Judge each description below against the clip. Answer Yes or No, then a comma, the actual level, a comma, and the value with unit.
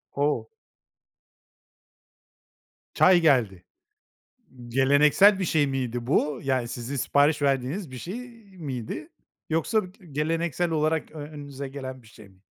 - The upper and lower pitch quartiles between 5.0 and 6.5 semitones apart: No, average, 3.5 semitones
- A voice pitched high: No, medium, 145 Hz